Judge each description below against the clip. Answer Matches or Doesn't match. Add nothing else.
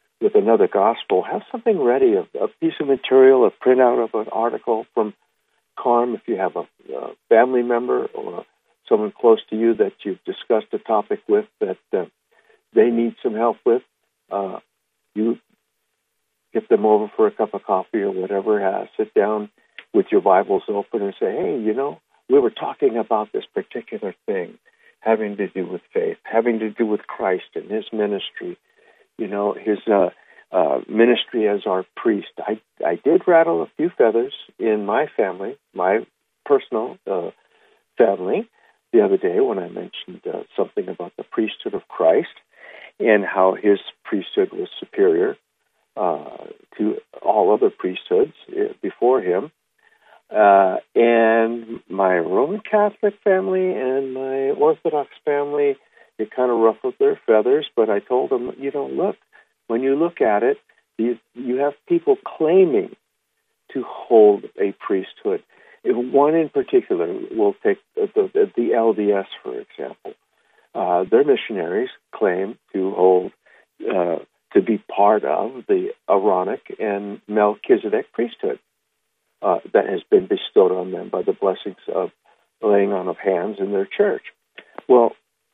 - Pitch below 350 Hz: Doesn't match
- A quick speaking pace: Doesn't match